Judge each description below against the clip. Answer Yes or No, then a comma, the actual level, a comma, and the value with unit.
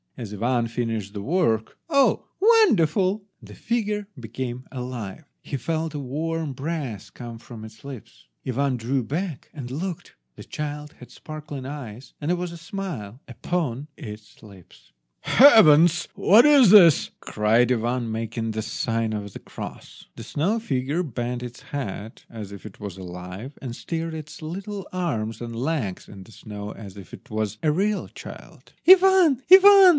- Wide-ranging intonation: Yes, wide, 6.9 semitones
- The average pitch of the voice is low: Yes, low, 130 Hz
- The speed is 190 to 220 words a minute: No, average, 160 wpm